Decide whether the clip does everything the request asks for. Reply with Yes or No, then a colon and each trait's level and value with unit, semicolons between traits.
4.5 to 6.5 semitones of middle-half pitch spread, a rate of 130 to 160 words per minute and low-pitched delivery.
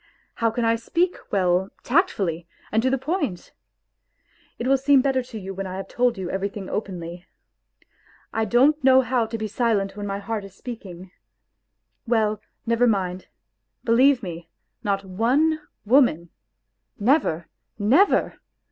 No: average, 4.9 semitones; average, 140 wpm; high, 220 Hz